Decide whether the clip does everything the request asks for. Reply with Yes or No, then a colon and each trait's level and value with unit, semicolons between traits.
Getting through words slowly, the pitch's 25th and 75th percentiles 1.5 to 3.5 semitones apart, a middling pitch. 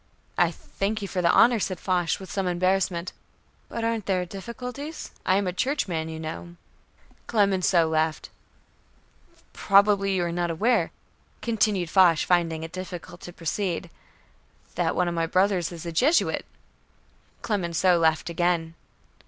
No: average, 145 wpm; average, 2.8 semitones; medium, 180 Hz